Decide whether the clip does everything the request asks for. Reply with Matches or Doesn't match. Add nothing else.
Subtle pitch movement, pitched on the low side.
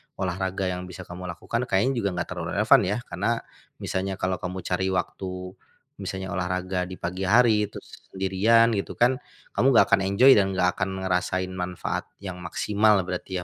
Matches